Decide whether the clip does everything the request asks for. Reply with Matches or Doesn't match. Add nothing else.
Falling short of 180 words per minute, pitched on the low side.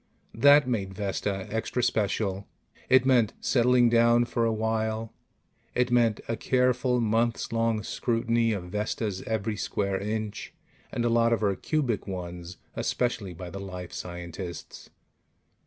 Matches